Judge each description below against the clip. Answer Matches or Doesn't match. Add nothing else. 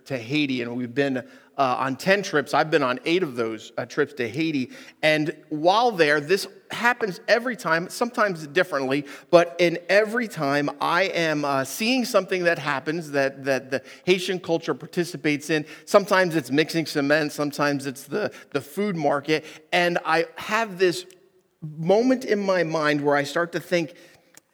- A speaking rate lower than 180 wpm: Matches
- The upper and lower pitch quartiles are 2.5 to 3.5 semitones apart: Doesn't match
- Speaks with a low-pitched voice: Doesn't match